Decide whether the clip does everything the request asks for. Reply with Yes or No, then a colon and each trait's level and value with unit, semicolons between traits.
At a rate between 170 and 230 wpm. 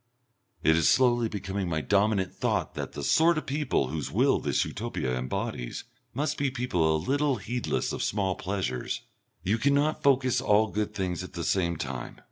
Yes: average, 175 wpm